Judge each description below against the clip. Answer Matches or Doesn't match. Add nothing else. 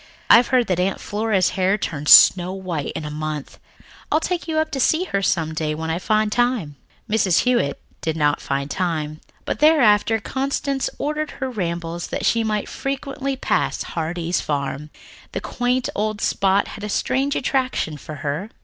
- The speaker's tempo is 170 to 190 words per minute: Matches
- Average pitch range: Doesn't match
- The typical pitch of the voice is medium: Doesn't match